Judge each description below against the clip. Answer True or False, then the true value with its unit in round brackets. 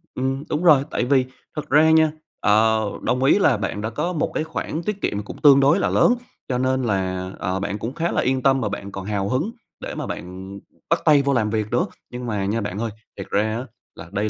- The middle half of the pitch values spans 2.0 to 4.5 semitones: False (5.5 semitones)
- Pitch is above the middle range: False (120 Hz)